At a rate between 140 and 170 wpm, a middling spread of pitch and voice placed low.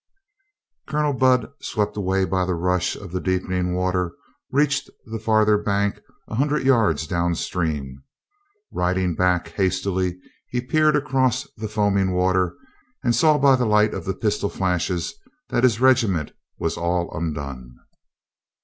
Yes: average, 145 wpm; average, 4.9 semitones; very low, 95 Hz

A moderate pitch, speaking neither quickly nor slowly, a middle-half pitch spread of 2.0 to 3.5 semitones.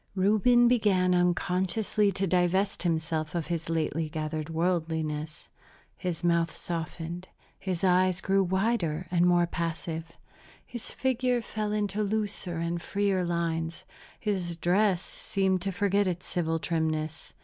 No: medium, 180 Hz; slow, 125 wpm; average, 3.0 semitones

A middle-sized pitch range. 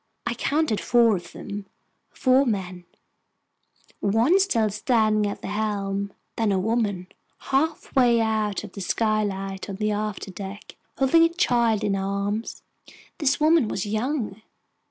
Yes: average, 3.3 semitones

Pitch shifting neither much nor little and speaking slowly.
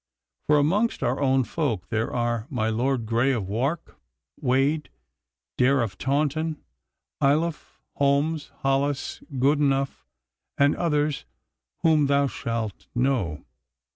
Yes: average, 3.7 semitones; slow, 110 wpm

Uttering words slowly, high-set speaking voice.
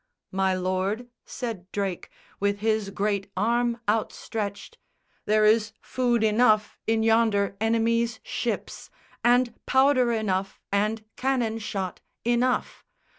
Yes: slow, 110 wpm; high, 220 Hz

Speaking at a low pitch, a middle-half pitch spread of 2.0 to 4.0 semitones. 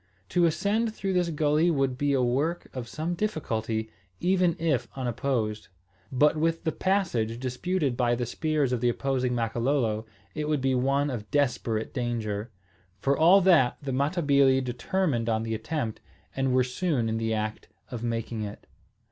No: low, 130 Hz; average, 5.1 semitones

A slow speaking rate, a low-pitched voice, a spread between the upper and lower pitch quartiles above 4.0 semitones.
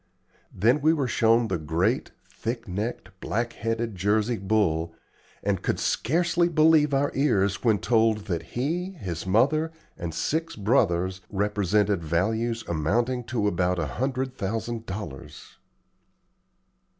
Yes: slow, 125 wpm; low, 110 Hz; average, 5.2 semitones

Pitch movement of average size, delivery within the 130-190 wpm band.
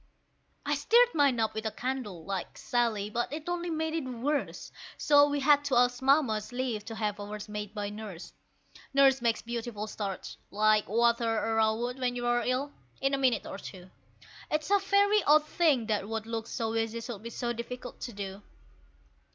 Yes: average, 4.3 semitones; average, 185 wpm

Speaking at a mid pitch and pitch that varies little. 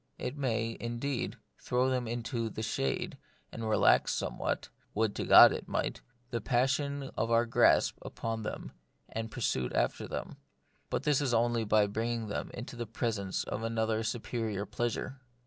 No: low, 115 Hz; narrow, 1.6 semitones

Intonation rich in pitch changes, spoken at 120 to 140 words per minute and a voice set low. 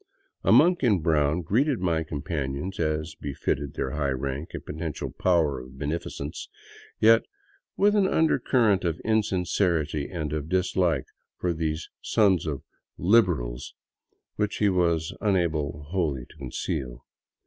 No: average, 4.5 semitones; slow, 135 wpm; very low, 80 Hz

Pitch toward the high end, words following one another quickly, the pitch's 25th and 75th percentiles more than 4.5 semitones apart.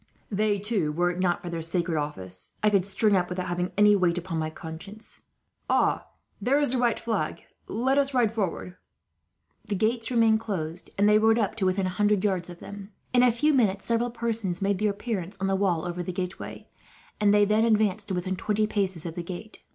No: high, 200 Hz; fast, 215 wpm; average, 3.6 semitones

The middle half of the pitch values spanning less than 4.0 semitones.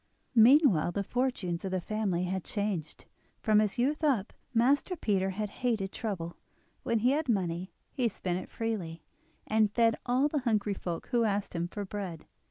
No: average, 4.4 semitones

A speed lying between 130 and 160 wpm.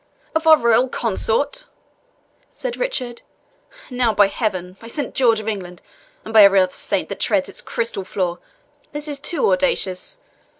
Yes: average, 155 wpm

